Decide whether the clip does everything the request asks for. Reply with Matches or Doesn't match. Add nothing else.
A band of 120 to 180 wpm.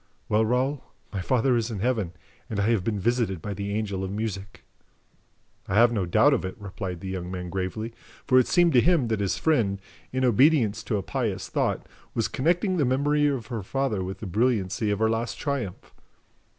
Doesn't match